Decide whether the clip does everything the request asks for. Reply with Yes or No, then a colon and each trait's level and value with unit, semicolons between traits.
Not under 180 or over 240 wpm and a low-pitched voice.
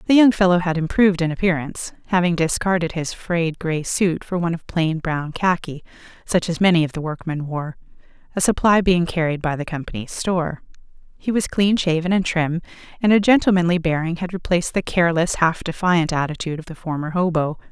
No: average, 185 wpm; medium, 170 Hz